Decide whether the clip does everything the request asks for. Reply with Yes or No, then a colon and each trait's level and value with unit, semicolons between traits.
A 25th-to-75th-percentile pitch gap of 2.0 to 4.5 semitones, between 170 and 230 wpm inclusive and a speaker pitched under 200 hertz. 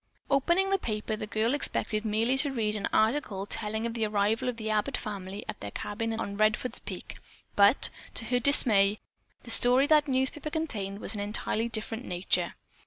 No: average, 3.4 semitones; average, 185 wpm; high, 220 Hz